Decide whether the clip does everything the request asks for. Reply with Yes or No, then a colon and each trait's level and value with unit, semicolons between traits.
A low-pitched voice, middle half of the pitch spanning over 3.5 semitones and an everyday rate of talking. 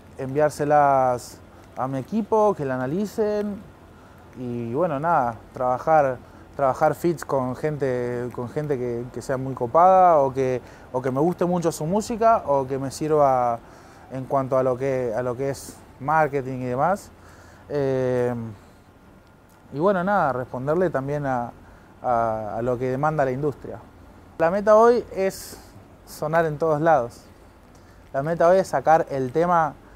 Yes: low, 130 Hz; average, 4.8 semitones; average, 150 wpm